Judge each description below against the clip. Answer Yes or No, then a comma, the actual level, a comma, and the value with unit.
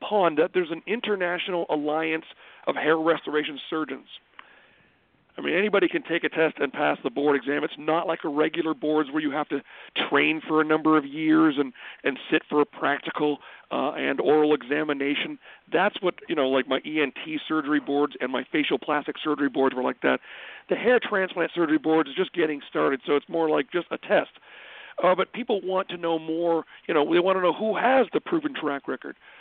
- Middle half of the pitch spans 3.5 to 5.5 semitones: No, average, 2.7 semitones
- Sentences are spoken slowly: No, fast, 205 wpm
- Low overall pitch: No, medium, 155 Hz